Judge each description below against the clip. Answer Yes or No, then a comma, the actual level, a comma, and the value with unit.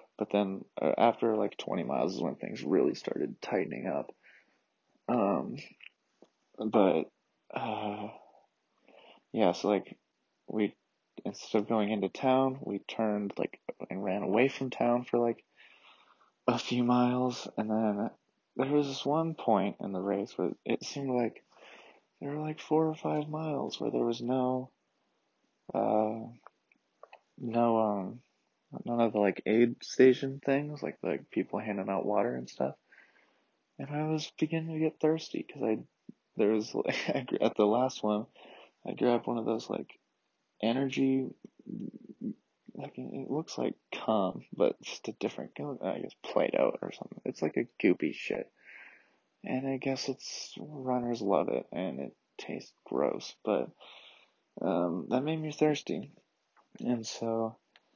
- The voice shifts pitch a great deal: No, average, 3.8 semitones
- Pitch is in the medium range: No, low, 125 Hz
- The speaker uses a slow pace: No, average, 150 wpm